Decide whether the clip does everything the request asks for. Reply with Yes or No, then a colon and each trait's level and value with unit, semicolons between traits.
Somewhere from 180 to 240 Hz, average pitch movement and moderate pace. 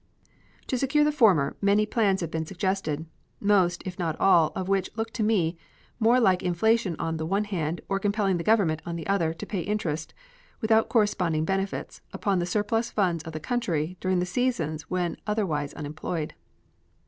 Yes: medium, 185 Hz; average, 4.4 semitones; average, 180 wpm